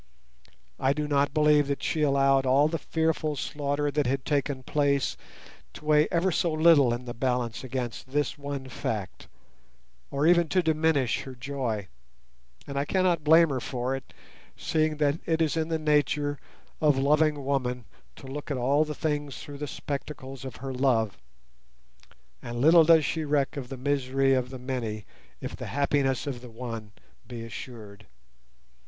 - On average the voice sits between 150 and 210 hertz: No, medium, 140 Hz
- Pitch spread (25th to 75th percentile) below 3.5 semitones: Yes, average, 2.9 semitones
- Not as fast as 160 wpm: No, average, 165 wpm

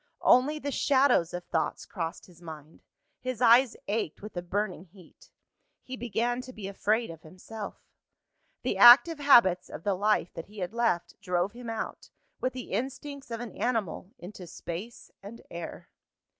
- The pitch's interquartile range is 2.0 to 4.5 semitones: No, wide, 5.4 semitones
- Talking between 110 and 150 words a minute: No, average, 165 wpm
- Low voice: No, high, 215 Hz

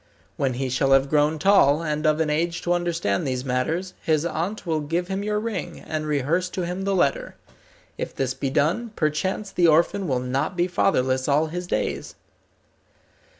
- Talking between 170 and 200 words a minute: Yes, average, 185 wpm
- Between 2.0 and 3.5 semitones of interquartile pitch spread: No, average, 4.3 semitones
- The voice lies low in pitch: No, medium, 160 Hz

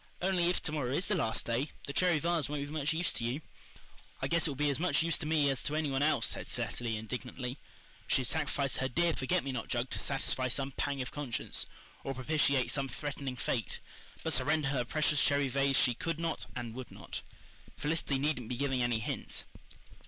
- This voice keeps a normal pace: No, fast, 220 wpm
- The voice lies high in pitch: No, medium, 140 Hz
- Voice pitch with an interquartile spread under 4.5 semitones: Yes, average, 3.3 semitones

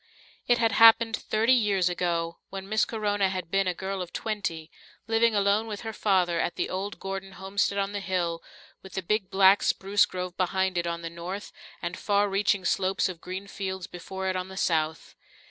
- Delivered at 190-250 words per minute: Yes, average, 195 wpm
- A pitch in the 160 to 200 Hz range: Yes, high, 190 Hz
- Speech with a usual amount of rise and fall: No, narrow, 2.1 semitones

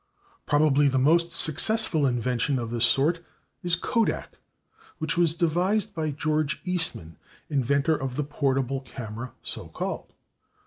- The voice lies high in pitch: No, medium, 145 Hz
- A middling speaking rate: No, slow, 130 wpm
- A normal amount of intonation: Yes, average, 4.1 semitones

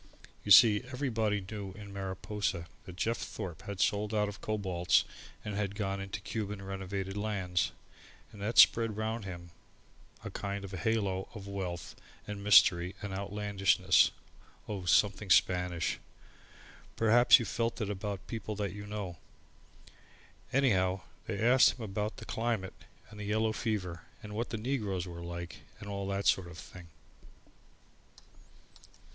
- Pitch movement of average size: No, narrow, 2.2 semitones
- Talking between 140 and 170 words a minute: Yes, average, 145 wpm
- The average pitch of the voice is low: Yes, low, 100 Hz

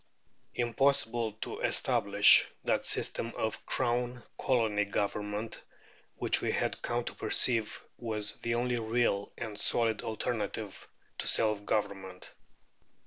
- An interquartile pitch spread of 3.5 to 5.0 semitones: No, narrow, 2.5 semitones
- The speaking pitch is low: Yes, low, 110 Hz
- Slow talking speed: Yes, slow, 115 wpm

